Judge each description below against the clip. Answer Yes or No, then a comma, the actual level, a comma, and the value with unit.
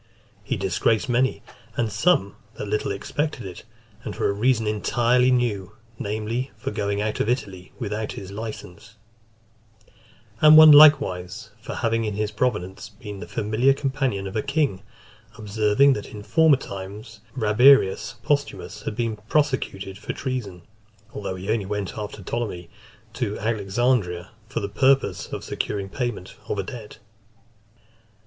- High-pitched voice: No, low, 110 Hz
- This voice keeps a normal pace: Yes, average, 145 wpm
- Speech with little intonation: No, average, 3.9 semitones